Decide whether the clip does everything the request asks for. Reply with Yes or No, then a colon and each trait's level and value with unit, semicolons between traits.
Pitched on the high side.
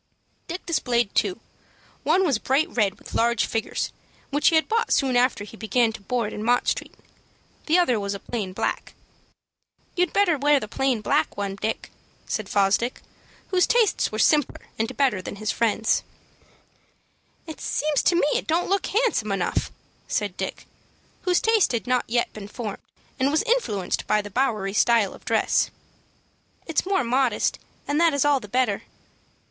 Yes: high, 245 Hz